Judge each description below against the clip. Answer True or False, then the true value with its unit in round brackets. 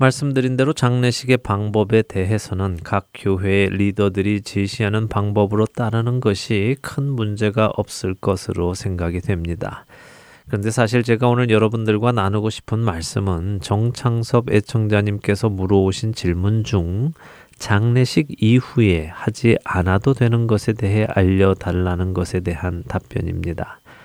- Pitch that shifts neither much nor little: True (3.0 semitones)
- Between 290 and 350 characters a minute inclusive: True (305 characters per minute)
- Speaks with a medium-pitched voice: False (105 Hz)